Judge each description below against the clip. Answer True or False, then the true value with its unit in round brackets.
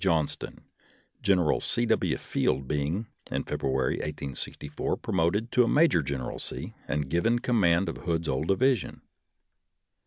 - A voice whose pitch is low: True (85 Hz)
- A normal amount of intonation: False (6.3 semitones)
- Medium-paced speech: False (125 wpm)